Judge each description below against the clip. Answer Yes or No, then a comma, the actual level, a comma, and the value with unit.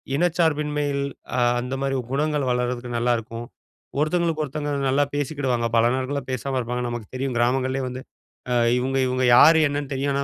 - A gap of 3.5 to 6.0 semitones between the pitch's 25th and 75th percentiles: No, average, 2.9 semitones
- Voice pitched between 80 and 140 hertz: Yes, low, 135 Hz